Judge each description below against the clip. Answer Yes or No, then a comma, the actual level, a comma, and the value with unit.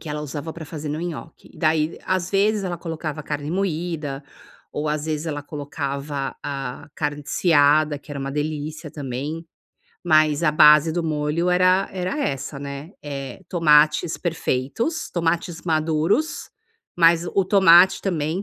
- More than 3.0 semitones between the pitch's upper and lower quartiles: No, narrow, 2.6 semitones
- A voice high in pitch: No, medium, 155 Hz